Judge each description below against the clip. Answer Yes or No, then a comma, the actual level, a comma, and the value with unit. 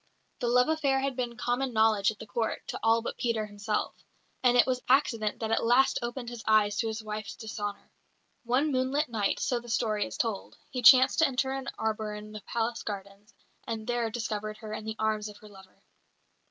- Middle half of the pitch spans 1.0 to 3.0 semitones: Yes, average, 2.7 semitones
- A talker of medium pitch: No, high, 225 Hz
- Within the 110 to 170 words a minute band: No, fast, 205 wpm